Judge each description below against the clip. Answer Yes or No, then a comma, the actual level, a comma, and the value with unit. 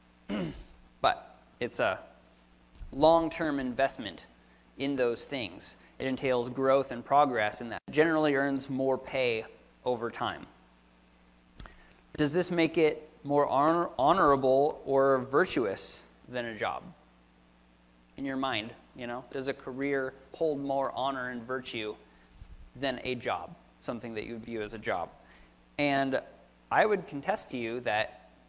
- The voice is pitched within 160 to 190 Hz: No, low, 125 Hz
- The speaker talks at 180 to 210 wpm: No, slow, 135 wpm